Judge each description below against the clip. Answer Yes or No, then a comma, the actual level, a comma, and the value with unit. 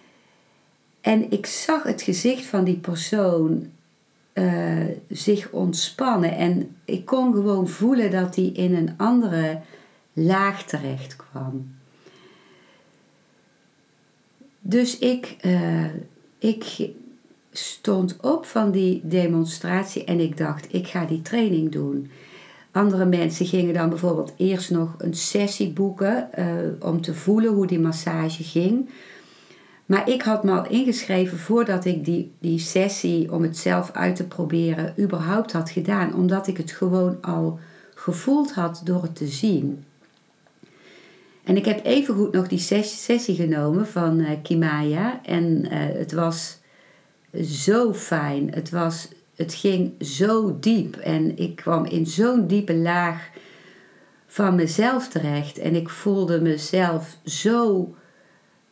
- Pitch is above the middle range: No, medium, 180 Hz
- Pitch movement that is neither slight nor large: Yes, average, 3.5 semitones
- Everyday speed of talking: No, slow, 130 wpm